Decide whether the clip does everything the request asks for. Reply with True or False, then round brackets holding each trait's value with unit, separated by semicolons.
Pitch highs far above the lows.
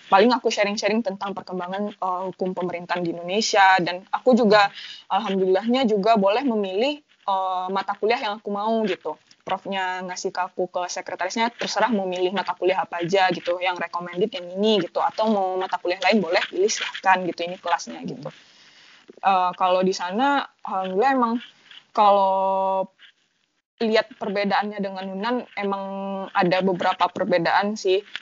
False (2.4 semitones)